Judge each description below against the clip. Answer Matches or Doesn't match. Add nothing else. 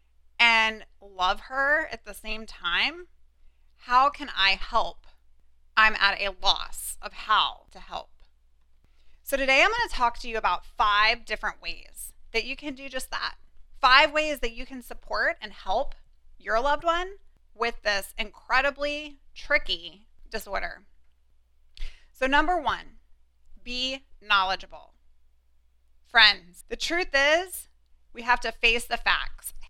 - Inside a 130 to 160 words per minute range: Matches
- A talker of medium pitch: Doesn't match